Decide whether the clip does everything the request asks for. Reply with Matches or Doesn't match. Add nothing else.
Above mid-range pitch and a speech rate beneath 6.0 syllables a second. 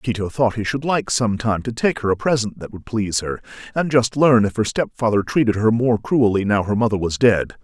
Doesn't match